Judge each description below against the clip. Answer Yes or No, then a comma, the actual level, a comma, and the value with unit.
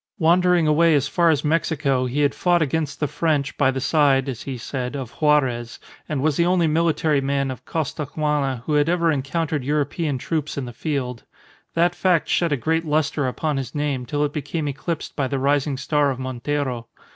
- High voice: No, medium, 145 Hz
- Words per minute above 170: Yes, average, 195 wpm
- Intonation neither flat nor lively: Yes, average, 3.0 semitones